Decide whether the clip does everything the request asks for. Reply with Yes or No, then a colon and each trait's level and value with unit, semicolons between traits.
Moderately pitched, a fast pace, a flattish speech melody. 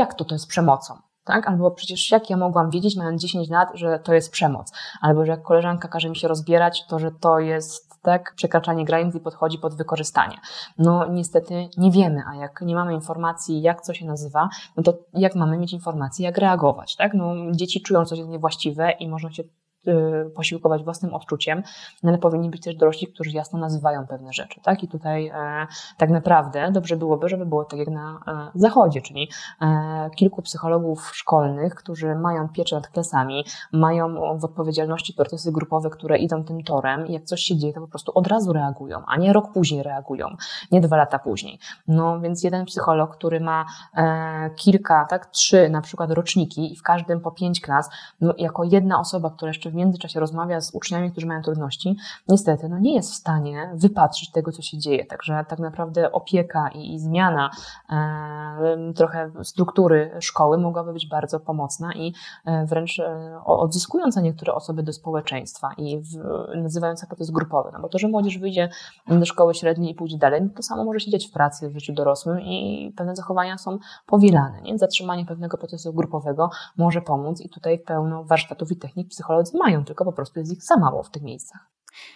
Yes: medium, 165 Hz; fast, 190 wpm; narrow, 2.0 semitones